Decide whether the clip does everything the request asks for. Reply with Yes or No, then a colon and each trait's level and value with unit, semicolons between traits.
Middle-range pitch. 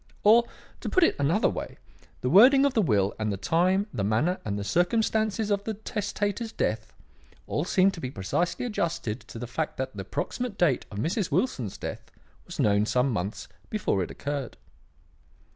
Yes: medium, 165 Hz